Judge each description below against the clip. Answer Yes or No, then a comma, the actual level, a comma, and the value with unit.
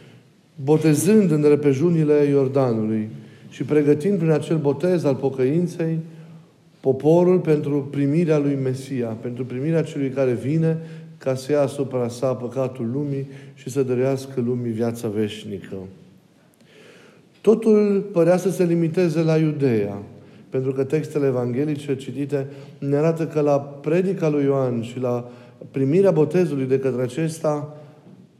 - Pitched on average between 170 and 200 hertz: No, medium, 145 Hz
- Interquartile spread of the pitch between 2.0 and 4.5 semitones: Yes, average, 3.5 semitones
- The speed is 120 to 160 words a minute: Yes, average, 125 wpm